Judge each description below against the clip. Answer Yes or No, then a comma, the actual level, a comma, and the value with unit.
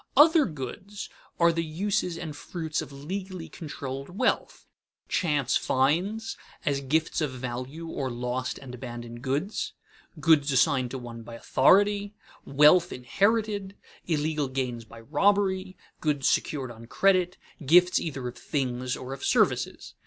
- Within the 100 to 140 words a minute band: Yes, slow, 135 wpm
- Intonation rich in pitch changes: Yes, wide, 6.0 semitones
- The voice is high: No, medium, 150 Hz